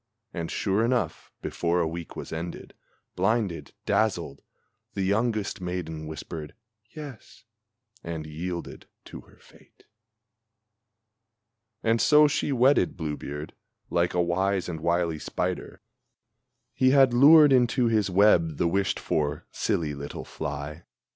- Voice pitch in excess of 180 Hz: No, very low, 90 Hz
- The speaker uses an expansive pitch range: Yes, wide, 5.9 semitones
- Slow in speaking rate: Yes, slow, 125 wpm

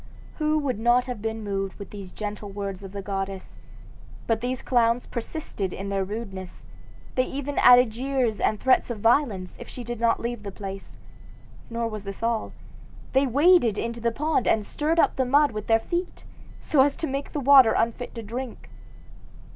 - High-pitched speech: Yes, high, 230 Hz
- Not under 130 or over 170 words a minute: No, average, 185 wpm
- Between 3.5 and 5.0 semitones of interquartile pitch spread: Yes, average, 4.2 semitones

